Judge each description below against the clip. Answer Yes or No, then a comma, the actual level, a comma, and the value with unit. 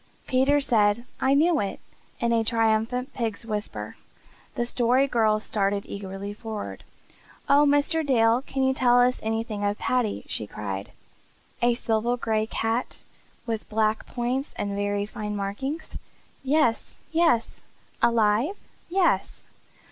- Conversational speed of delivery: No, slow, 130 wpm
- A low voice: No, high, 230 Hz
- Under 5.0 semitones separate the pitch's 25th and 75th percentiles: Yes, average, 3.8 semitones